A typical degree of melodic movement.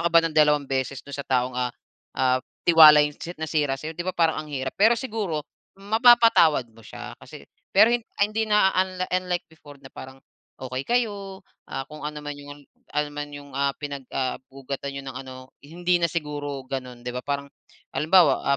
Yes: average, 4.5 semitones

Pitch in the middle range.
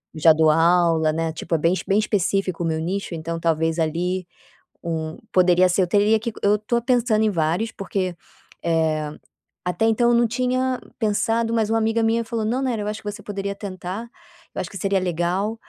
No: high, 195 Hz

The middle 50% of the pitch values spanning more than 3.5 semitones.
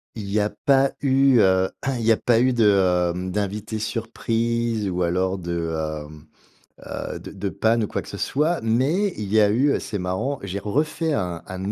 Yes: average, 4.4 semitones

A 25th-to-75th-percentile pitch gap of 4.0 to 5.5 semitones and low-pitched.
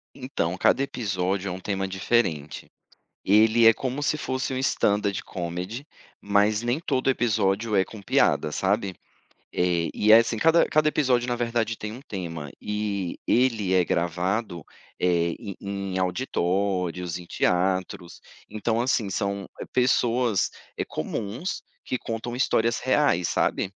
Yes: average, 4.6 semitones; low, 105 Hz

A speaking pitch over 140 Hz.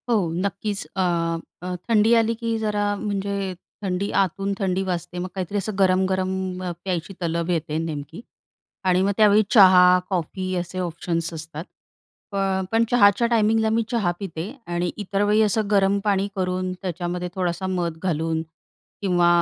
Yes: high, 190 Hz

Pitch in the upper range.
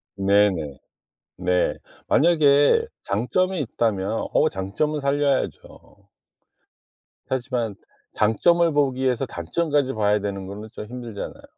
No: low, 120 Hz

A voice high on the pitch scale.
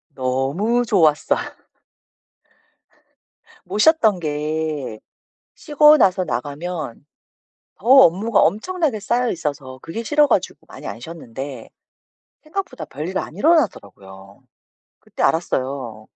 No: medium, 165 Hz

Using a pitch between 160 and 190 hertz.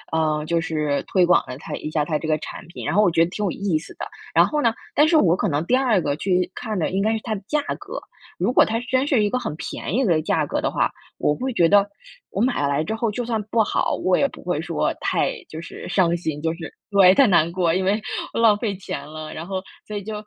Yes: medium, 185 Hz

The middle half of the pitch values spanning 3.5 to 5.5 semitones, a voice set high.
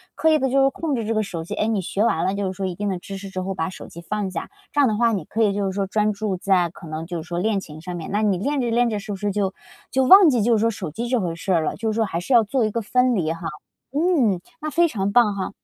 Yes: average, 3.9 semitones; high, 205 Hz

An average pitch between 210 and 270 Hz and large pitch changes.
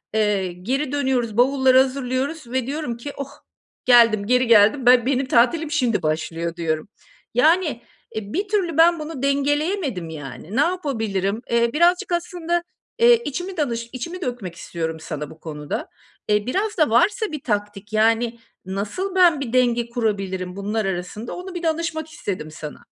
Yes: high, 245 Hz; wide, 7.1 semitones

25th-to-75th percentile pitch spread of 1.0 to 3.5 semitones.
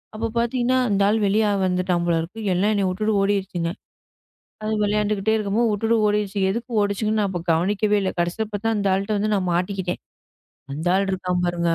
Yes: average, 2.7 semitones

